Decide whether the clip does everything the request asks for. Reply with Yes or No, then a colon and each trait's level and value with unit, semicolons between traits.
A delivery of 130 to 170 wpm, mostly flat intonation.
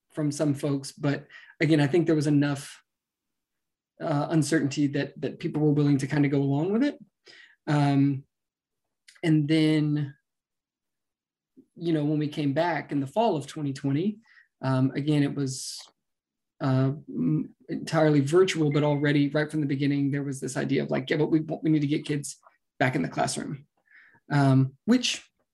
Yes: average, 165 wpm; narrow, 1.8 semitones